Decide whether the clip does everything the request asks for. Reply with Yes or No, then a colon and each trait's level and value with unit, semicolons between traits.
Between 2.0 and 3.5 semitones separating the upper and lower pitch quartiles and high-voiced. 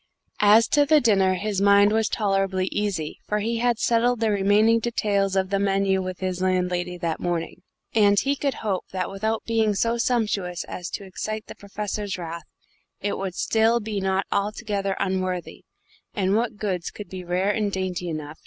Yes: average, 2.7 semitones; high, 200 Hz